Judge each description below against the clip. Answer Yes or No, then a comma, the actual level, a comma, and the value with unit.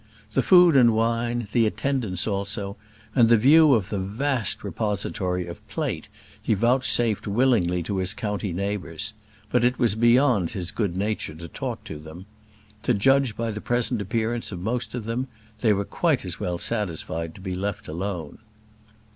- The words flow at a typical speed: Yes, average, 170 wpm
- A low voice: Yes, low, 105 Hz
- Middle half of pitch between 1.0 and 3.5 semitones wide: No, average, 4.2 semitones